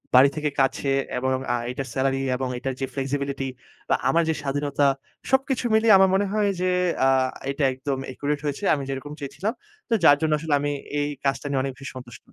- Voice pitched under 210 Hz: Yes, medium, 140 Hz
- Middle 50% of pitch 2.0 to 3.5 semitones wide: Yes, average, 2.8 semitones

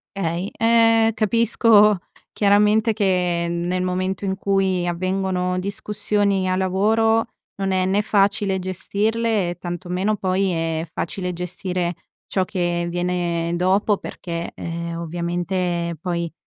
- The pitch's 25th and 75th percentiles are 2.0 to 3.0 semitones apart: Yes, narrow, 2.6 semitones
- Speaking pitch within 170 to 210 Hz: Yes, medium, 185 Hz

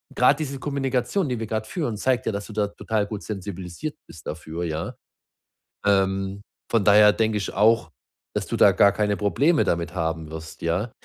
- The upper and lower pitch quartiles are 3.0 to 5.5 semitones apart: Yes, average, 3.9 semitones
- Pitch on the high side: No, low, 105 Hz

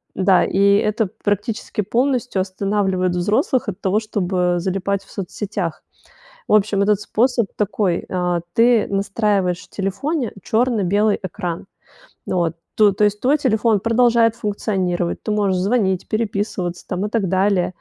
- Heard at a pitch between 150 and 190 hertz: No, high, 205 Hz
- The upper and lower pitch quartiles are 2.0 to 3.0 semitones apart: Yes, average, 2.7 semitones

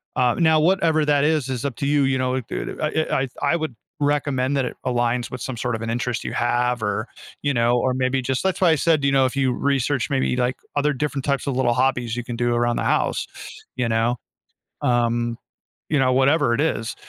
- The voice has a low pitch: Yes, low, 130 Hz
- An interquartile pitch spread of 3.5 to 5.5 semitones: No, average, 2.9 semitones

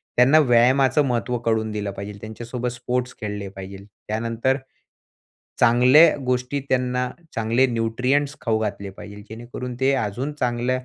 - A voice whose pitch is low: Yes, low, 120 Hz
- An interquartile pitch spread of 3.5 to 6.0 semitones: No, narrow, 2.5 semitones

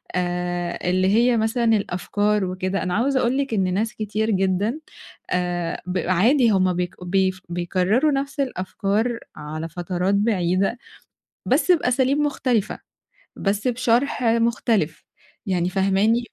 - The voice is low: No, high, 200 Hz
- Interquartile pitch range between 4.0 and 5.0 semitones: Yes, average, 4.4 semitones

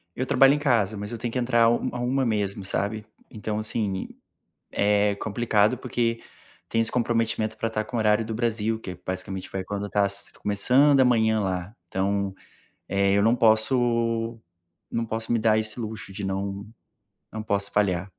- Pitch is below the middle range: Yes, low, 110 Hz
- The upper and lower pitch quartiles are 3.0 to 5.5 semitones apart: No, narrow, 2.4 semitones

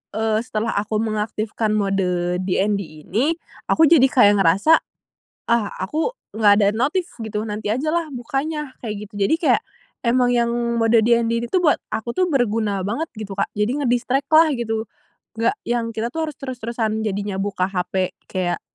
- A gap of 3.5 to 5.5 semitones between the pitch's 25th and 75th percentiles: Yes, average, 3.9 semitones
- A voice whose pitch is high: Yes, high, 225 Hz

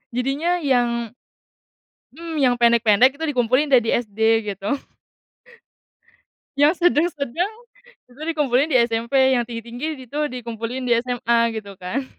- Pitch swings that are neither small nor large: Yes, average, 3.5 semitones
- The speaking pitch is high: Yes, high, 245 Hz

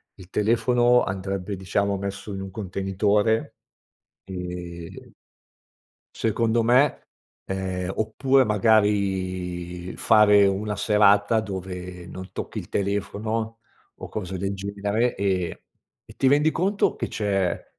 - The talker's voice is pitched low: Yes, low, 100 Hz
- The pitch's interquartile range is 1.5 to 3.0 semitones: Yes, narrow, 2.6 semitones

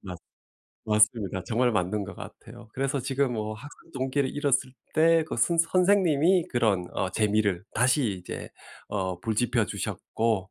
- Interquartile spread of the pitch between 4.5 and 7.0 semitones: Yes, average, 5.3 semitones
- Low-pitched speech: Yes, low, 115 Hz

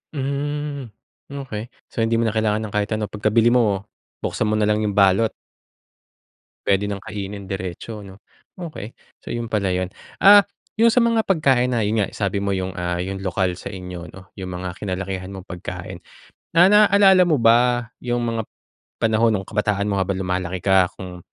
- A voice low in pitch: Yes, low, 105 Hz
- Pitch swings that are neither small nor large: Yes, average, 4.1 semitones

